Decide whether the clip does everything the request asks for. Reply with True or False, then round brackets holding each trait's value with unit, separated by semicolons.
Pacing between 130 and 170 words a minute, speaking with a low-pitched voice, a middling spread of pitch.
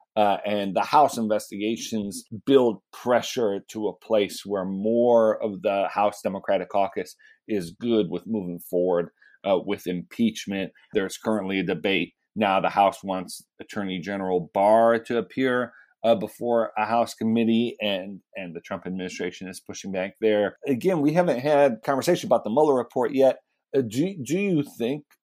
True (160 wpm; 105 Hz; 3.5 semitones)